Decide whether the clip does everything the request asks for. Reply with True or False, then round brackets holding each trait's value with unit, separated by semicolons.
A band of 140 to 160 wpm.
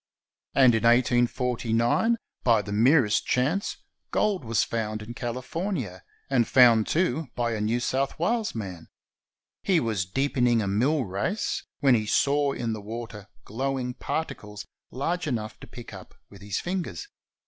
True (150 wpm)